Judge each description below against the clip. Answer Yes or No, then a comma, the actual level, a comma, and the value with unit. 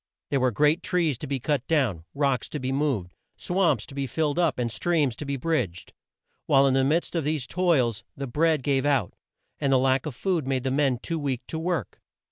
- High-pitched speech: No, medium, 140 Hz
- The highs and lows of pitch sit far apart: No, average, 3.5 semitones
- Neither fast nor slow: No, fast, 220 wpm